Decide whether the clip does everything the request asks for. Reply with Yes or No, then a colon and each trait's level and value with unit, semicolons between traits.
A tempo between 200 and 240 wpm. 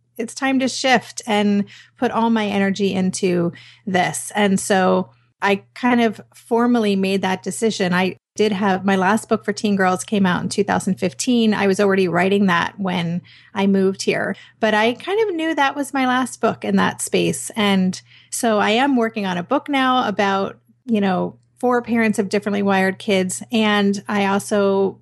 No: average, 180 wpm